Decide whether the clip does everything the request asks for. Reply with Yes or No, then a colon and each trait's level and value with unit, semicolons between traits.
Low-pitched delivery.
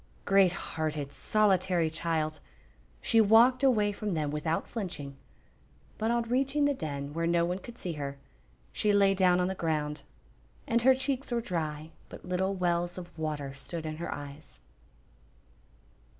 No: medium, 175 Hz